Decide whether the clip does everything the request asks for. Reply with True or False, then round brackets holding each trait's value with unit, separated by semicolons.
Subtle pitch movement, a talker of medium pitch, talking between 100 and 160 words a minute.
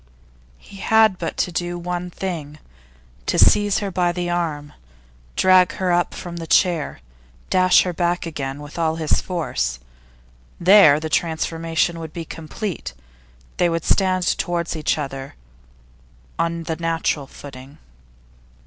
True (2.2 semitones; 170 Hz; 140 wpm)